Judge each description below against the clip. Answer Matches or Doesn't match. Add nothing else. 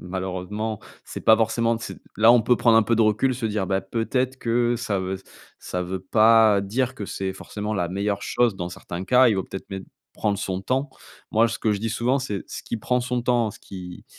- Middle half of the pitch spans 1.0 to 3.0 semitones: Doesn't match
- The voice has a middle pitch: Doesn't match